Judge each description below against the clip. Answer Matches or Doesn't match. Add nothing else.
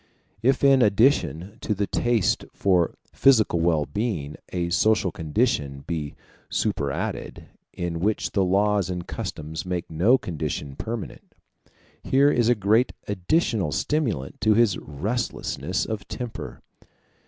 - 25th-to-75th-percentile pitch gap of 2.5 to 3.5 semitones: Doesn't match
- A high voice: Doesn't match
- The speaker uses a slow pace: Matches